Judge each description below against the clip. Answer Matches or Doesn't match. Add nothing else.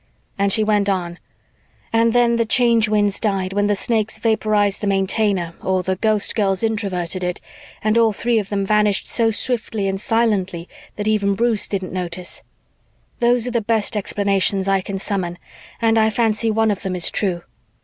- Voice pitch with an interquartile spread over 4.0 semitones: Doesn't match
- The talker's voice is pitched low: Doesn't match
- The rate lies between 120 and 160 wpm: Doesn't match